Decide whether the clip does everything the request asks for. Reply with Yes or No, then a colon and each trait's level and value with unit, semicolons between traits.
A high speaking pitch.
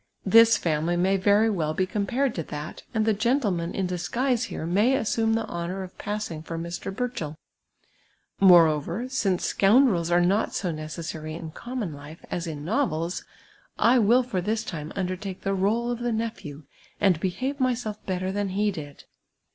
Yes: high, 195 Hz